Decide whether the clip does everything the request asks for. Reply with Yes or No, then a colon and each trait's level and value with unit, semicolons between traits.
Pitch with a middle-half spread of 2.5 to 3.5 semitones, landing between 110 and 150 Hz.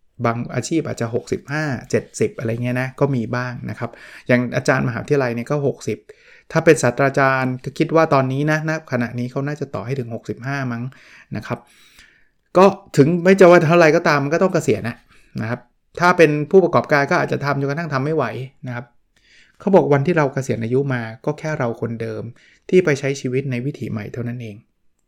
No: average, 4.3 semitones; low, 135 Hz